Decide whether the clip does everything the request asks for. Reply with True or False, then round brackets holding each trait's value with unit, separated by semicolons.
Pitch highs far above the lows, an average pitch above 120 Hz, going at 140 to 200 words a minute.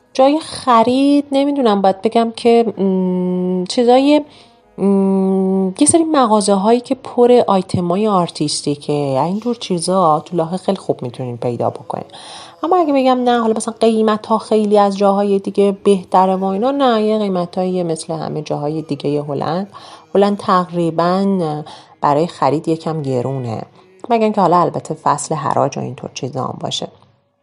True (5.8 semitones; 190 Hz; 150 wpm)